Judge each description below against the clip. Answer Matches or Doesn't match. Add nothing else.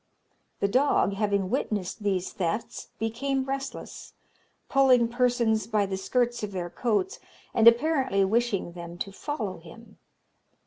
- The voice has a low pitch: Doesn't match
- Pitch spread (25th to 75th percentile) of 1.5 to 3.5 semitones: Doesn't match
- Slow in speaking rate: Matches